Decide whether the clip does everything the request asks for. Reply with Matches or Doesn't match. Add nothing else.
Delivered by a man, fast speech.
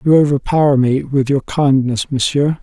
Doesn't match